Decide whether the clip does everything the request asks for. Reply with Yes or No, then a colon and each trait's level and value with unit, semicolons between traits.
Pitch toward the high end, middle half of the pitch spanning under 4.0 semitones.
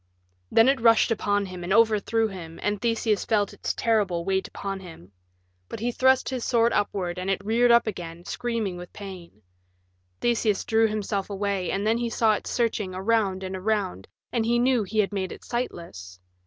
Yes: high, 205 Hz; average, 3.4 semitones